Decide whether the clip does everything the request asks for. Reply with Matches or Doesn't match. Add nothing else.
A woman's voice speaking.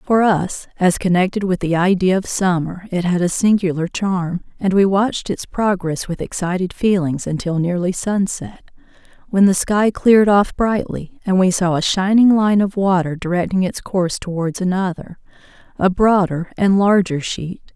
Matches